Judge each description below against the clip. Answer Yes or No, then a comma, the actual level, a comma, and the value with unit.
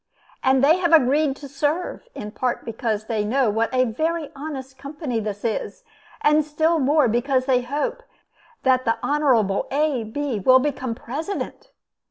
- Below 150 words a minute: No, average, 160 wpm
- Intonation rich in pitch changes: No, average, 4.1 semitones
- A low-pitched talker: No, very high, 265 Hz